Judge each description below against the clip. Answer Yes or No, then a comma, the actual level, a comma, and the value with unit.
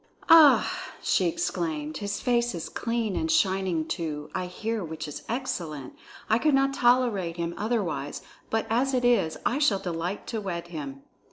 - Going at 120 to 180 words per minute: Yes, average, 165 wpm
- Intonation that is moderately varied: No, wide, 6.6 semitones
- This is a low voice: No, high, 195 Hz